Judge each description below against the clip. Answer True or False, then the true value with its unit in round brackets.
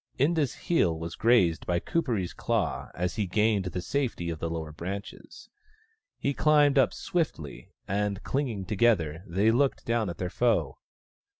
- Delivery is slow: False (155 wpm)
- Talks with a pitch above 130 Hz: False (100 Hz)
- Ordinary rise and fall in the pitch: False (6.3 semitones)